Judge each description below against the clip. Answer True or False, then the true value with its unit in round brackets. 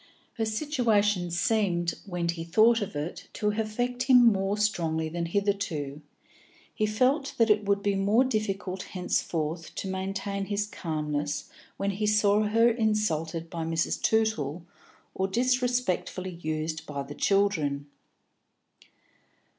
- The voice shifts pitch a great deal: False (4.5 semitones)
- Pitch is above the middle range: True (195 Hz)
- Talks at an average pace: False (130 wpm)